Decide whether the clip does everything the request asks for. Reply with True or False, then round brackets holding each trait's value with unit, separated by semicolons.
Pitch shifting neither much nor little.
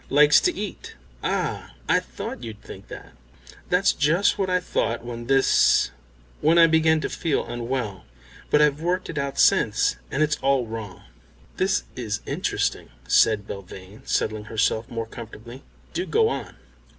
False (6.3 semitones)